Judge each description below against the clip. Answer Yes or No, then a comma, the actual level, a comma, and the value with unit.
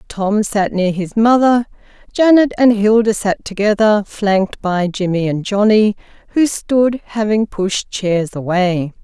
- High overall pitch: Yes, high, 205 Hz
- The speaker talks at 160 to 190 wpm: No, average, 140 wpm